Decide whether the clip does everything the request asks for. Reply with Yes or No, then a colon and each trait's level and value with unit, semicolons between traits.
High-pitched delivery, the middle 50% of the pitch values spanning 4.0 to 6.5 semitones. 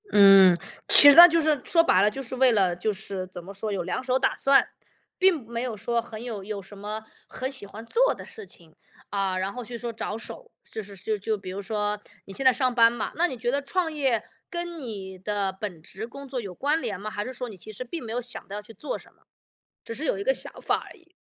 Yes: high, 225 Hz; average, 4.8 semitones